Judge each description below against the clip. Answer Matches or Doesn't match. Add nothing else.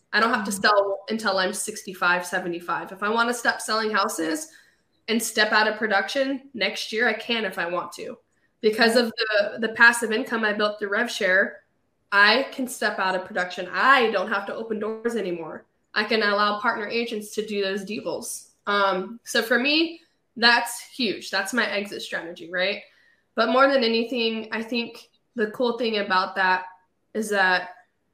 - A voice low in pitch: Doesn't match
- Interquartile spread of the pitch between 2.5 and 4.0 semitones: Matches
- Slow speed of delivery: Doesn't match